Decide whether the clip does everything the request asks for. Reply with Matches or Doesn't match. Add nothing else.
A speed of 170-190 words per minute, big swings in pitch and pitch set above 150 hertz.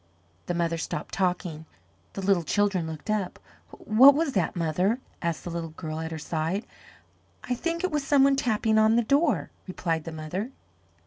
Matches